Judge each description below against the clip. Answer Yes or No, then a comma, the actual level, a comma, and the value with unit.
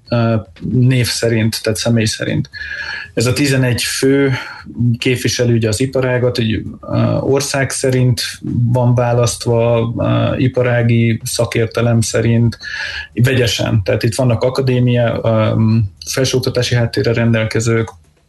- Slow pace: Yes, slow, 90 wpm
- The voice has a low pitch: Yes, low, 120 Hz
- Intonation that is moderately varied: No, narrow, 1.8 semitones